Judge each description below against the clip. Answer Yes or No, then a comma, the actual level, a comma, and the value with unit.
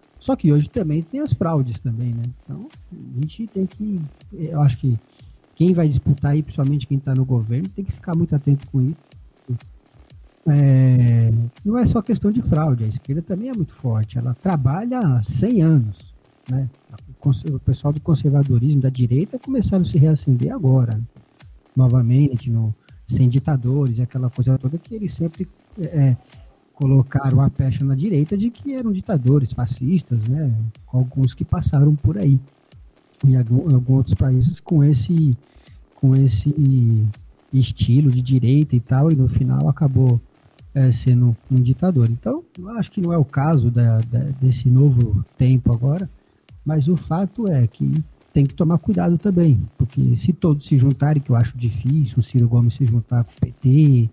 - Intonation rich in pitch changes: No, average, 3.8 semitones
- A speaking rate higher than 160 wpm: Yes, average, 170 wpm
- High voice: No, low, 135 Hz